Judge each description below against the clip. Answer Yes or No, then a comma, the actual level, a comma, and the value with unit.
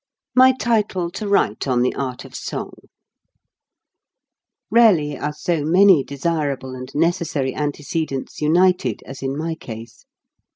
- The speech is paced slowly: Yes, slow, 130 wpm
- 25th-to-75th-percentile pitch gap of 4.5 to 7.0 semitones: Yes, average, 5.2 semitones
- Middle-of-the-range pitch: Yes, medium, 150 Hz